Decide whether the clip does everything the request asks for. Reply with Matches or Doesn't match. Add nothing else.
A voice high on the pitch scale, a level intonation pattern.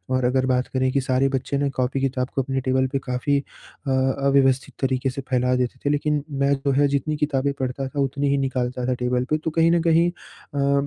Doesn't match